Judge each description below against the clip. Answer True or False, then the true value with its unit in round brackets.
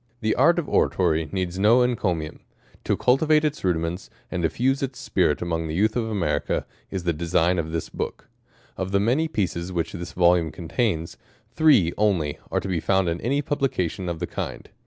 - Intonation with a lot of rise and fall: True (6.2 semitones)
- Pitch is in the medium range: False (95 Hz)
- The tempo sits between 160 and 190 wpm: True (185 wpm)